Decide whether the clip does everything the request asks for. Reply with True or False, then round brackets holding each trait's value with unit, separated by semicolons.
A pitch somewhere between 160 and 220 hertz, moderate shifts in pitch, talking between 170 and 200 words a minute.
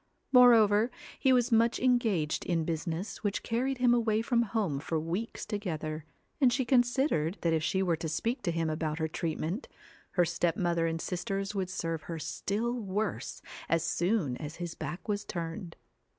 False (185 Hz; 5.7 semitones; 175 wpm)